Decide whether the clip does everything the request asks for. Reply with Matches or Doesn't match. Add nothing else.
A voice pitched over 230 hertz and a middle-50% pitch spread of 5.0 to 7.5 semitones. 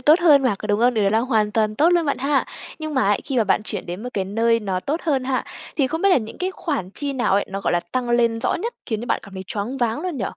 Matches